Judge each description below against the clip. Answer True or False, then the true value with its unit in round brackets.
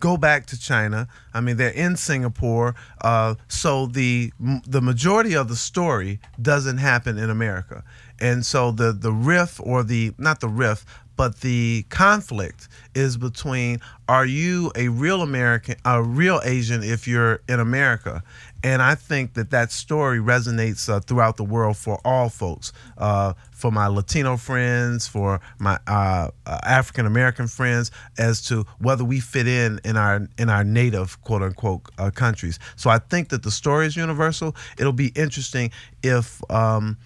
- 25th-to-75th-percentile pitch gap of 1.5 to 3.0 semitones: True (2.7 semitones)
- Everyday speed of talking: True (165 wpm)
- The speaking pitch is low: True (120 Hz)